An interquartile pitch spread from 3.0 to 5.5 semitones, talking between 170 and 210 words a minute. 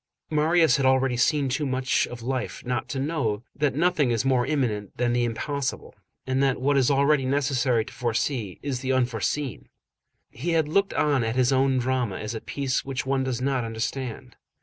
No: narrow, 2.4 semitones; average, 195 wpm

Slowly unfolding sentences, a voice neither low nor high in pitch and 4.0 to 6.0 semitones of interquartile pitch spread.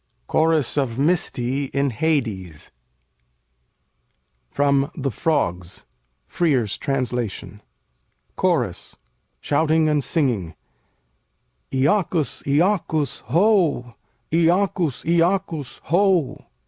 Yes: slow, 70 wpm; medium, 145 Hz; average, 5.1 semitones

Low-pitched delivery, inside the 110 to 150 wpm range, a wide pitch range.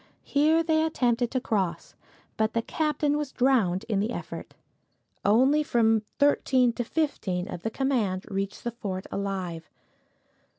No: high, 230 Hz; average, 140 wpm; wide, 6.2 semitones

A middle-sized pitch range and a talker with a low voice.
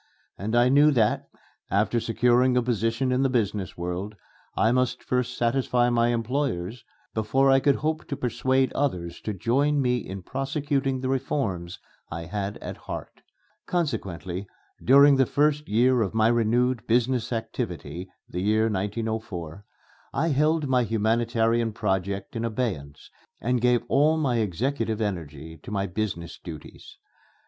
Yes: average, 4.5 semitones; low, 115 Hz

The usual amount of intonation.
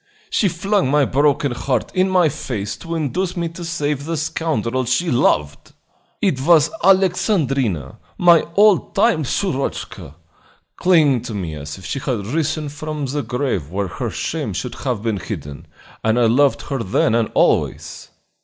No: wide, 6.2 semitones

